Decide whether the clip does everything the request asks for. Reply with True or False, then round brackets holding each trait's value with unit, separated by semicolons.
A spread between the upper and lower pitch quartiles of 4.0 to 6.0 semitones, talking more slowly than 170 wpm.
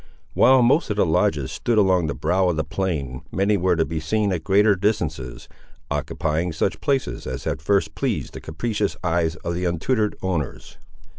False (4.5 semitones; 180 wpm)